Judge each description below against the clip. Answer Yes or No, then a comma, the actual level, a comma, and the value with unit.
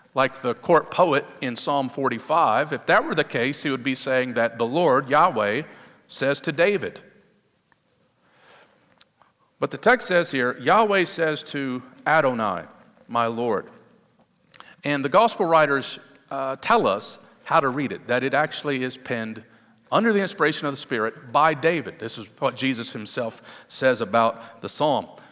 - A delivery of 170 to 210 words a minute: No, average, 160 wpm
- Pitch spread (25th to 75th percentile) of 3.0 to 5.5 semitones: Yes, average, 4.0 semitones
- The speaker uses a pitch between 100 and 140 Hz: Yes, low, 135 Hz